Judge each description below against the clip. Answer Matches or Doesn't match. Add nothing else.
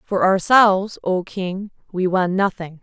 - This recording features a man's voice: Doesn't match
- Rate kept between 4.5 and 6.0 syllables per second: Doesn't match